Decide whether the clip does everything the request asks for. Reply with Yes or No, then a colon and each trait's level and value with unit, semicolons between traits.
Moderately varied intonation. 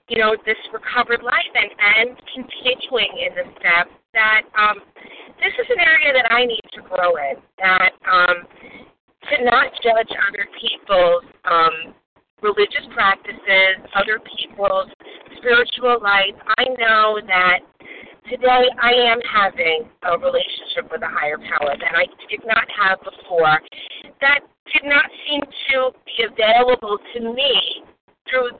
Yes: average, 4.6 semitones